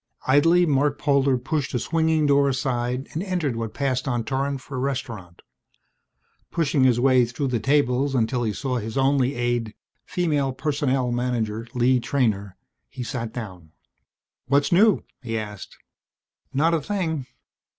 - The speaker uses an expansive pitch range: No, average, 2.9 semitones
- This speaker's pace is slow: No, average, 150 wpm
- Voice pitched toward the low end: Yes, low, 130 Hz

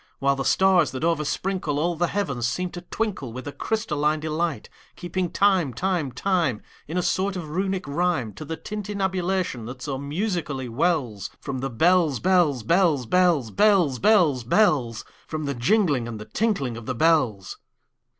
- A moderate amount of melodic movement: No, wide, 5.9 semitones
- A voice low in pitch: No, medium, 160 Hz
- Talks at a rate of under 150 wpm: Yes, average, 140 wpm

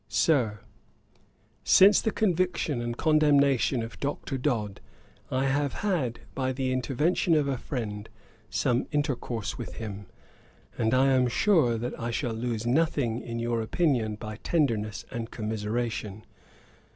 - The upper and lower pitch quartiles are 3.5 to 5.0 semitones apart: Yes, average, 4.2 semitones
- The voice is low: Yes, low, 125 Hz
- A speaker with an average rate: No, slow, 130 wpm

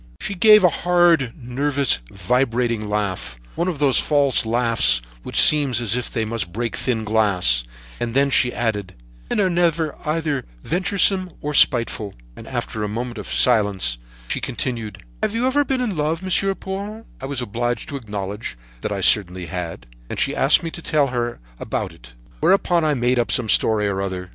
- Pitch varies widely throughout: Yes, wide, 7.1 semitones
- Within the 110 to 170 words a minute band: No, average, 180 wpm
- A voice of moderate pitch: No, low, 125 Hz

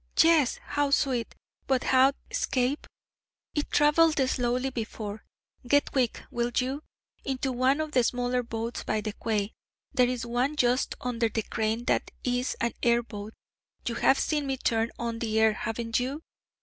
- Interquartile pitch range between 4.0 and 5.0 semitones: No, narrow, 2.6 semitones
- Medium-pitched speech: No, high, 245 Hz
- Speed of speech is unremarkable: Yes, average, 160 wpm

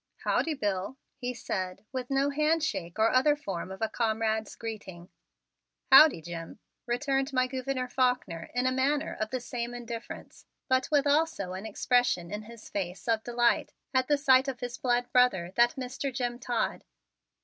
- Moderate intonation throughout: Yes, average, 3.5 semitones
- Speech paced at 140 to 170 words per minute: Yes, average, 165 wpm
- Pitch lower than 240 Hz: No, high, 245 Hz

